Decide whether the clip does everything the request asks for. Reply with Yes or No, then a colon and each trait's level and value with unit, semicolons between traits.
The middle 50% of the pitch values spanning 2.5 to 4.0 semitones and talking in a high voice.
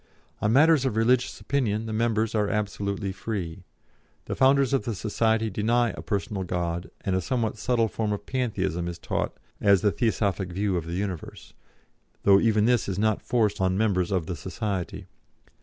No: average, 3.1 semitones; low, 105 Hz